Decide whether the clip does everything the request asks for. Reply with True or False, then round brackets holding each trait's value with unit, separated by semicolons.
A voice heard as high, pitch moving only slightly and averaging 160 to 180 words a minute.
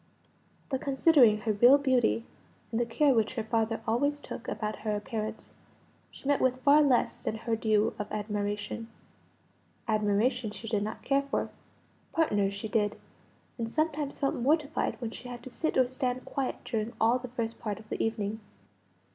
False (230 Hz; 3.5 semitones; 170 wpm)